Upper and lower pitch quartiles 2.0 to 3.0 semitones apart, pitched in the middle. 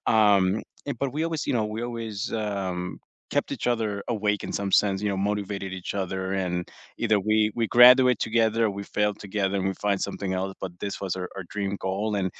No: narrow, 2.5 semitones; low, 105 Hz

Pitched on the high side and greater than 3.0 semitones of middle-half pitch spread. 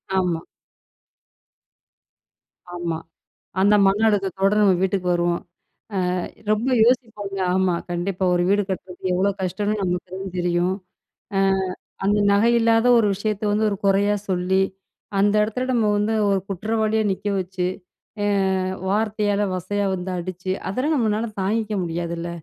No: high, 195 Hz; average, 2.7 semitones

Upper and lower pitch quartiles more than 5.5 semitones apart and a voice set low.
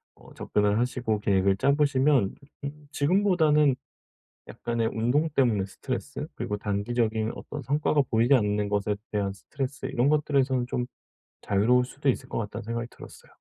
No: average, 5.2 semitones; low, 120 Hz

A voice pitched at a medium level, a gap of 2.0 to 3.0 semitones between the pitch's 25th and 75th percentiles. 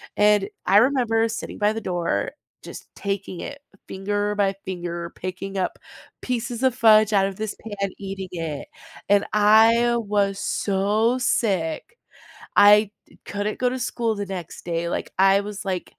No: high, 205 Hz; narrow, 2.6 semitones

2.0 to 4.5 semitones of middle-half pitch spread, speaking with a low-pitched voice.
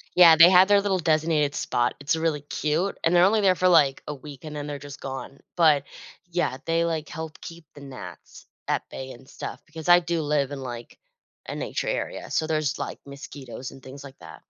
No: average, 3.3 semitones; medium, 155 Hz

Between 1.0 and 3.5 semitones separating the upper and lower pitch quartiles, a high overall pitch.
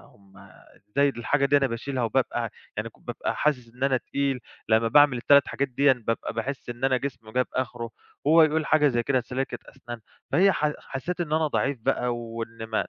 No: average, 3.2 semitones; low, 130 Hz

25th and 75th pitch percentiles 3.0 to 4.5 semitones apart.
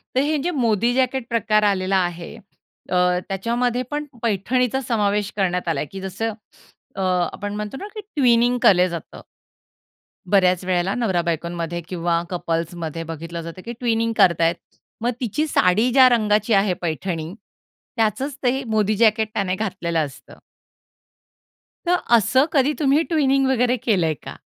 No: wide, 5.6 semitones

